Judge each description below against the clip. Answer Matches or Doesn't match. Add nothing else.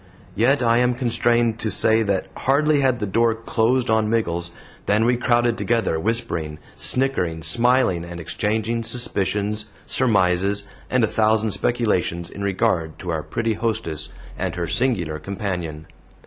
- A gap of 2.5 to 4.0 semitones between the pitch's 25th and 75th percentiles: Doesn't match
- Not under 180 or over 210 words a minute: Doesn't match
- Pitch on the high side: Doesn't match